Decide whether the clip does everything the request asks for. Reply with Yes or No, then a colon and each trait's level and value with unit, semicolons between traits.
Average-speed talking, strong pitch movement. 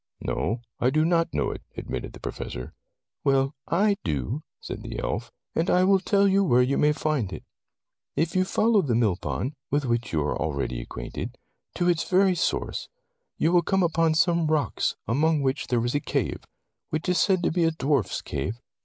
Yes: average, 195 wpm; wide, 6.5 semitones